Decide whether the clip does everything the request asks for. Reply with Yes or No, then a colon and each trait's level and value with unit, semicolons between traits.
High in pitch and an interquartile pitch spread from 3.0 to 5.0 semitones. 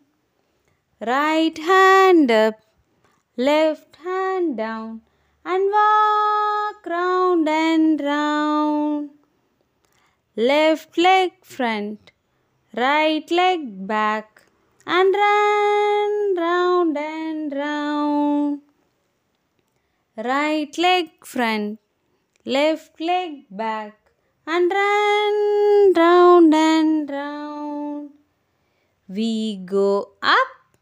Yes: very high, 310 Hz; average, 4.3 semitones